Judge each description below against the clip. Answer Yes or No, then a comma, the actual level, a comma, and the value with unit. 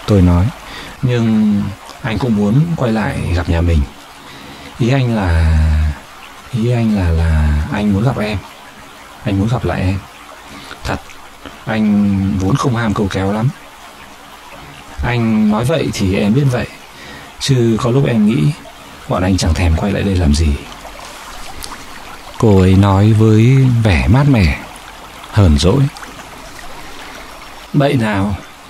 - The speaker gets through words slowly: Yes, slow, 140 wpm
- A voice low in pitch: Yes, very low, 95 Hz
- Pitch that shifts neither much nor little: No, wide, 7.4 semitones